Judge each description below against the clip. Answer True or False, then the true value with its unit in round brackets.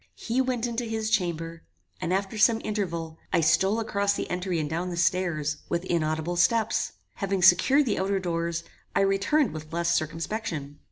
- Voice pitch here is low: False (180 Hz)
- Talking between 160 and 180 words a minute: True (170 wpm)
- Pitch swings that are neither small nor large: True (4.4 semitones)